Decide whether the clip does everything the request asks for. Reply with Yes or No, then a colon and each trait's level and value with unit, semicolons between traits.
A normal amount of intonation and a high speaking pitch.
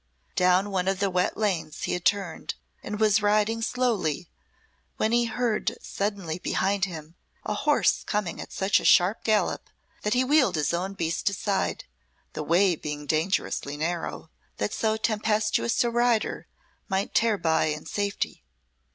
Yes: average, 3.8 semitones; high, 200 Hz